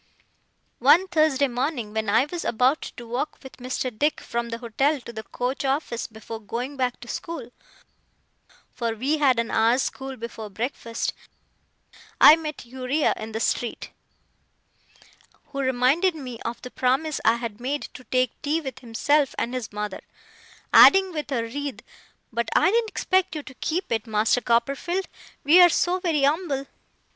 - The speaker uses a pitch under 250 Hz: No, very high, 255 Hz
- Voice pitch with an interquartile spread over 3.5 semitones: Yes, average, 4.3 semitones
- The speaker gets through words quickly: No, average, 160 wpm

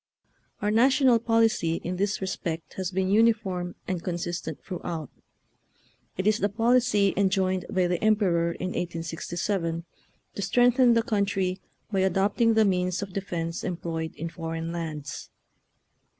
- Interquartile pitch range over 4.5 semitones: No, average, 3.7 semitones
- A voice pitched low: No, high, 190 Hz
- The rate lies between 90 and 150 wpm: Yes, average, 145 wpm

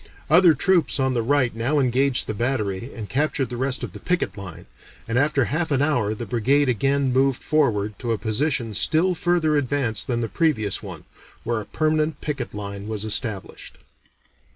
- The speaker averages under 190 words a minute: Yes, average, 180 wpm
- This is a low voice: Yes, low, 130 Hz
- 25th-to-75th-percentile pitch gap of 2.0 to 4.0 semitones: No, average, 4.8 semitones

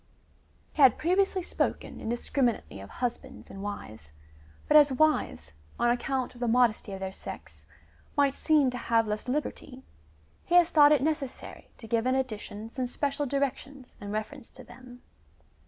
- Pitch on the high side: Yes, very high, 255 Hz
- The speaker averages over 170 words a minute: No, average, 165 wpm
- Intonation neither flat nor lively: Yes, average, 4.0 semitones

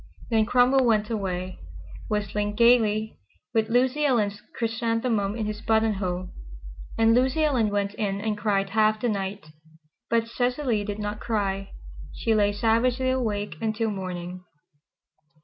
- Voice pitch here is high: Yes, high, 215 Hz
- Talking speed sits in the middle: No, slow, 130 wpm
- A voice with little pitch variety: Yes, narrow, 2.3 semitones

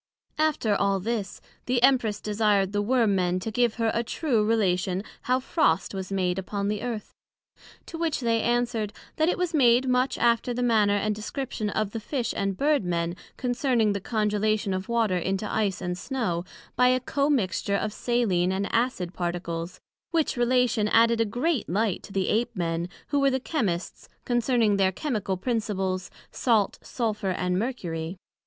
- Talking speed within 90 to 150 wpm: No, average, 170 wpm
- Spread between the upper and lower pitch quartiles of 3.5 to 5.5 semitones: Yes, average, 4.2 semitones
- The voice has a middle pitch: No, high, 215 Hz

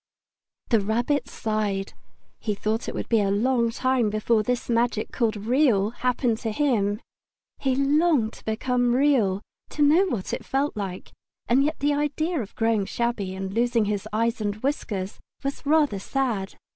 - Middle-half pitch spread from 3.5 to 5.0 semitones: Yes, average, 4.3 semitones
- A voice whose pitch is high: Yes, high, 235 Hz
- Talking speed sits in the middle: Yes, average, 165 wpm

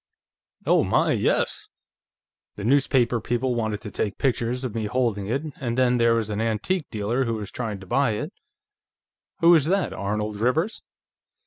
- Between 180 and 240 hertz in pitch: No, low, 115 Hz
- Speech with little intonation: No, average, 3.4 semitones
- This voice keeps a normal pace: Yes, average, 175 wpm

